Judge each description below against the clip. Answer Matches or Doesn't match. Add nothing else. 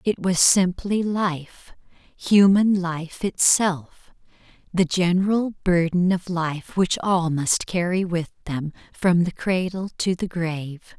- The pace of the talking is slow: Matches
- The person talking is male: Doesn't match